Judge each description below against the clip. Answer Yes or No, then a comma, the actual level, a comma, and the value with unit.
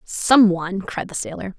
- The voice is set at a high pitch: Yes, high, 195 Hz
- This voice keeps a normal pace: Yes, average, 190 wpm